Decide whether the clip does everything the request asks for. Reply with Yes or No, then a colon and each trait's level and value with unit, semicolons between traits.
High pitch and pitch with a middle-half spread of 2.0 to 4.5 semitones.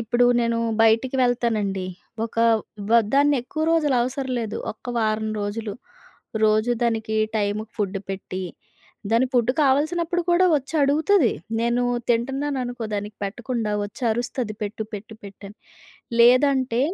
Yes: high, 235 Hz; average, 3.6 semitones